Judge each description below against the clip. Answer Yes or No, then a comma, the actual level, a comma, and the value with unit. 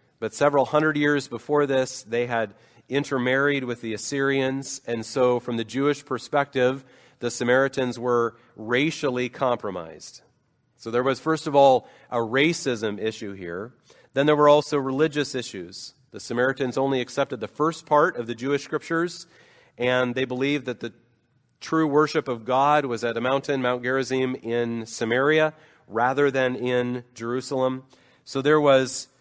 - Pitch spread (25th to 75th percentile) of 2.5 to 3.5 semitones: Yes, average, 2.9 semitones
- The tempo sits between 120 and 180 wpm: Yes, average, 150 wpm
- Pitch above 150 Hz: No, low, 130 Hz